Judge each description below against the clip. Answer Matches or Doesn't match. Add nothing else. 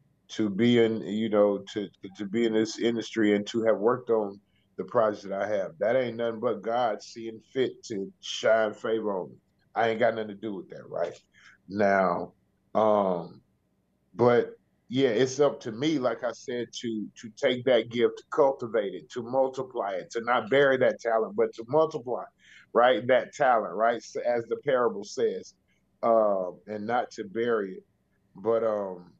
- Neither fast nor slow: Matches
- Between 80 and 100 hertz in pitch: Doesn't match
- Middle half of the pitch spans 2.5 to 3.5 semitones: Matches